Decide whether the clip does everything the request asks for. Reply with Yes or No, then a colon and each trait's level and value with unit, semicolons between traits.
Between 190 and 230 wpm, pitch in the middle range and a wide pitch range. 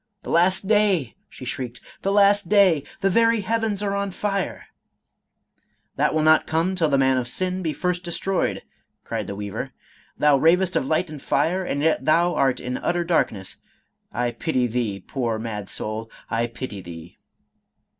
Yes: average, 200 wpm; medium, 160 Hz; wide, 7.4 semitones